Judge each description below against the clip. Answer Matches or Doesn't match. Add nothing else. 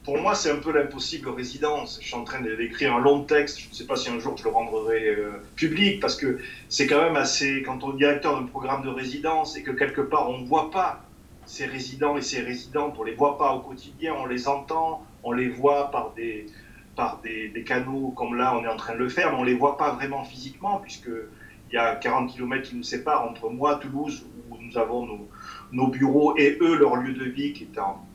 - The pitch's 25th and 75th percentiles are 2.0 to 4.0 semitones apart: Matches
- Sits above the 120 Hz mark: Matches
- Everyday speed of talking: Doesn't match